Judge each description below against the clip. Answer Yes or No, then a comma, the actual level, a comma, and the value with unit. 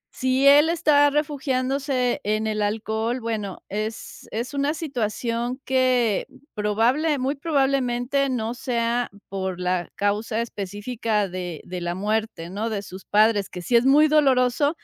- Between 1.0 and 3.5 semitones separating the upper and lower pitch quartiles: No, average, 4.3 semitones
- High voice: Yes, high, 235 Hz